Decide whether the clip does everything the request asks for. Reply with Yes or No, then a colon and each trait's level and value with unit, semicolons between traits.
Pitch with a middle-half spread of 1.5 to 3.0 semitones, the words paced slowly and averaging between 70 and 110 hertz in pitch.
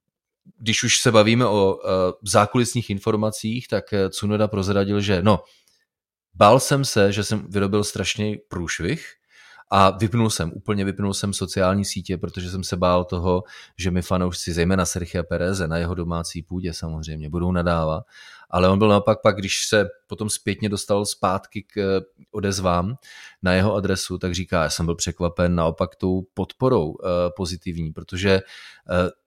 No: narrow, 2.6 semitones; average, 150 wpm; very low, 95 Hz